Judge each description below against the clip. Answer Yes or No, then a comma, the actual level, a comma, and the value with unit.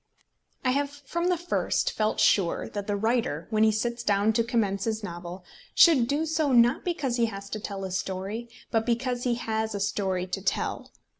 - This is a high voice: Yes, high, 220 Hz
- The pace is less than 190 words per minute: No, average, 200 wpm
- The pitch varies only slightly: No, average, 3.7 semitones